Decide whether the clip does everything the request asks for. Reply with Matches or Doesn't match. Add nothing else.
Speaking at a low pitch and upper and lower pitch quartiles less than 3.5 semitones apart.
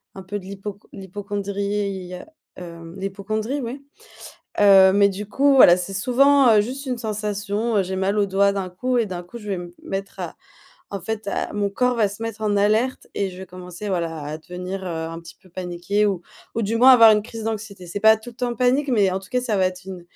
Doesn't match